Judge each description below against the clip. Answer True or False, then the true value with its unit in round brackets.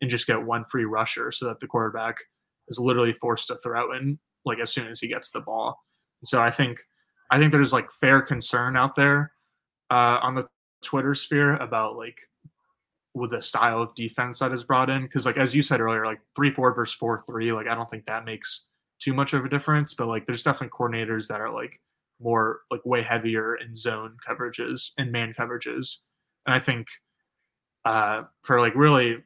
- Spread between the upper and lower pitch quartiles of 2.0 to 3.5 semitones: True (2.9 semitones)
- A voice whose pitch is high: False (125 Hz)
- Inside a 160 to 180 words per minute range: False (205 wpm)